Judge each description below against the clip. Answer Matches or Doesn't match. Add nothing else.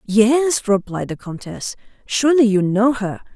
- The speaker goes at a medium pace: Matches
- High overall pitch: Matches